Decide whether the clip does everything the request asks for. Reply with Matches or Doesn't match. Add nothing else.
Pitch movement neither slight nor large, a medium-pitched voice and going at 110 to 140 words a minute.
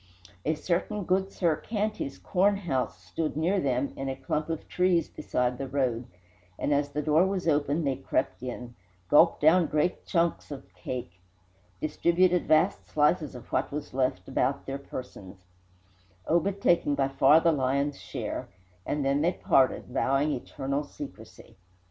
Doesn't match